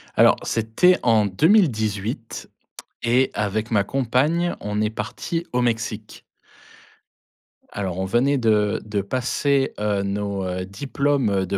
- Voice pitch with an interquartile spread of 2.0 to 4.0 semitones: No, average, 4.5 semitones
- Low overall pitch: Yes, low, 110 Hz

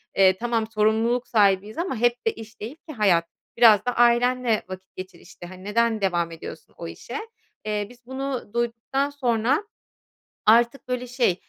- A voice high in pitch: Yes, high, 230 Hz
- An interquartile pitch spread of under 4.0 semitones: Yes, average, 3.1 semitones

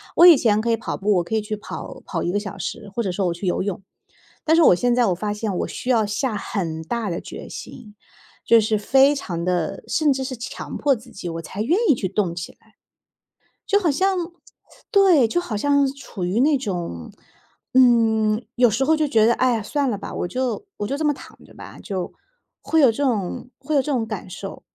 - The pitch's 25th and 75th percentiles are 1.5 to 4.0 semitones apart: No, average, 5.3 semitones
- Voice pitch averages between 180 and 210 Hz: No, high, 225 Hz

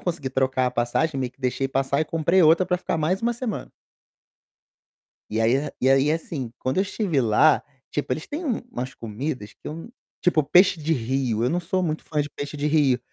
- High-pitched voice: No, medium, 150 Hz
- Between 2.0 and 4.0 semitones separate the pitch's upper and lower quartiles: No, average, 4.7 semitones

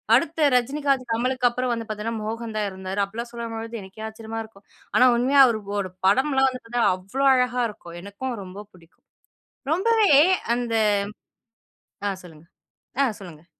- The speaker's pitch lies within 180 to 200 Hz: No, high, 230 Hz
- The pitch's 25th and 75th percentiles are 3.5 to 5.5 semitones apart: Yes, average, 3.9 semitones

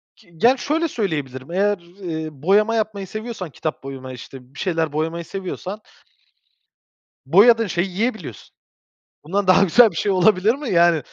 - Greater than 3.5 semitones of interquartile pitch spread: Yes, average, 5.1 semitones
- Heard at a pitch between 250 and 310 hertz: No, medium, 185 Hz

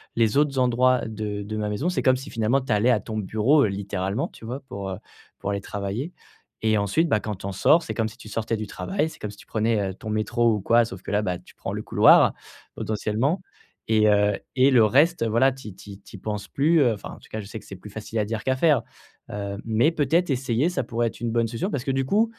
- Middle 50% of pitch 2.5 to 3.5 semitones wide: No, average, 4.0 semitones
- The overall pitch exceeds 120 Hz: No, low, 115 Hz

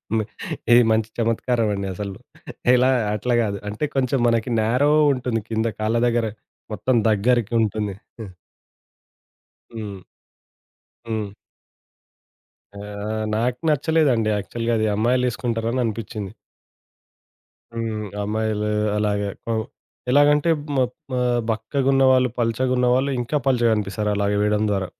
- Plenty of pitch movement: No, average, 2.8 semitones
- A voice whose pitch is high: No, low, 115 Hz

